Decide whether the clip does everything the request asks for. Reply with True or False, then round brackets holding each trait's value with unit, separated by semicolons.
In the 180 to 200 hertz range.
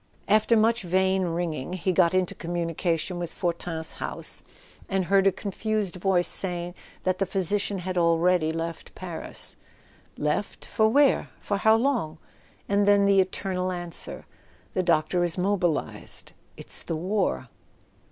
True (185 Hz)